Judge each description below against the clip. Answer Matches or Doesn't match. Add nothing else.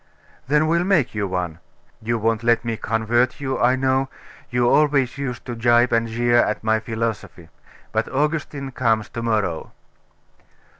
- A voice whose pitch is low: Matches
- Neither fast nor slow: Matches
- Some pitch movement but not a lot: Matches